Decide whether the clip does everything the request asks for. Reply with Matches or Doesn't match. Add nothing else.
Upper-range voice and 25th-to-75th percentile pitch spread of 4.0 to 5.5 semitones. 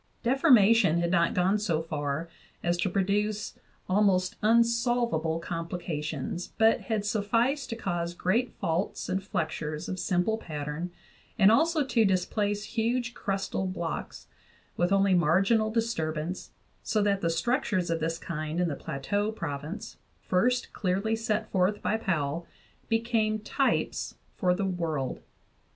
Matches